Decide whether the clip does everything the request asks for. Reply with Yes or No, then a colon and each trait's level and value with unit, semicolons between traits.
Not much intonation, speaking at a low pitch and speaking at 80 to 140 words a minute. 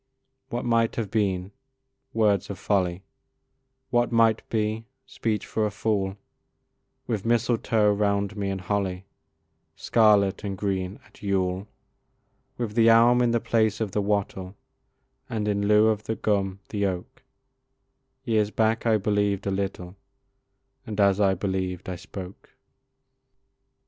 Yes: narrow, 2.3 semitones; low, 105 Hz; slow, 135 wpm